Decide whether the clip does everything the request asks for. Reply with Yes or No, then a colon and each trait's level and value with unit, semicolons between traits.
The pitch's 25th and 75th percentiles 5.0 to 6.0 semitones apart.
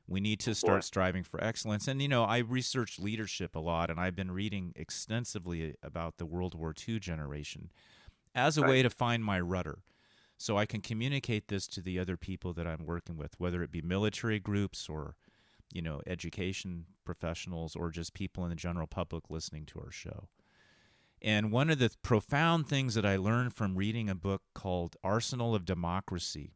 No: average, 4.3 semitones